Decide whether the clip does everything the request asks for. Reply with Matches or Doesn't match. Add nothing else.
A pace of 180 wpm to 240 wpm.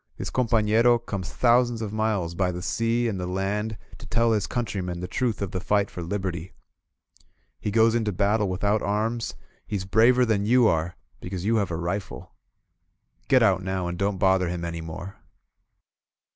Matches